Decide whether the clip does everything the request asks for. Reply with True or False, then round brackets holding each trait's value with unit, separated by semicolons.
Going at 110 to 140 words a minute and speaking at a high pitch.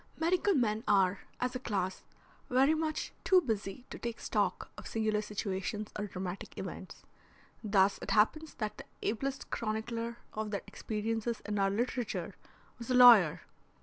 False (150 wpm; 220 Hz)